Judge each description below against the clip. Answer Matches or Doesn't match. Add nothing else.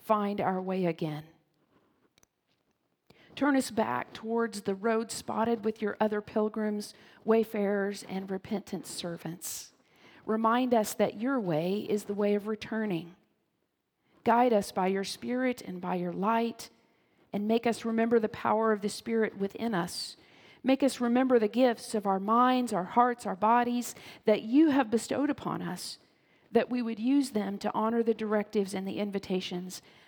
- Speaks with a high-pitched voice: Matches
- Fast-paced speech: Doesn't match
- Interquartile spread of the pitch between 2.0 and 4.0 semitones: Matches